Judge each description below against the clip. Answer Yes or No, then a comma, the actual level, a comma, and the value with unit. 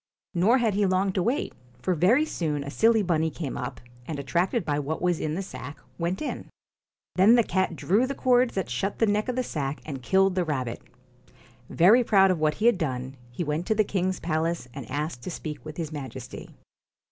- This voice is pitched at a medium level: Yes, medium, 175 Hz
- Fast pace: Yes, fast, 215 wpm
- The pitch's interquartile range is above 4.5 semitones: Yes, average, 5.1 semitones